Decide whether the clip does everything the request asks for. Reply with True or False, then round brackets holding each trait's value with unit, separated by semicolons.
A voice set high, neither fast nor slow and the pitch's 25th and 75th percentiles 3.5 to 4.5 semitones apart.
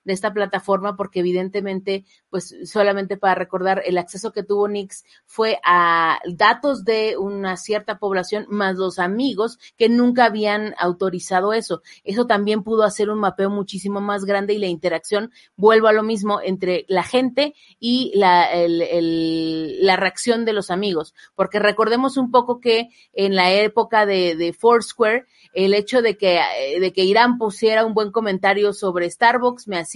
False (200 Hz; 165 wpm; 3.0 semitones)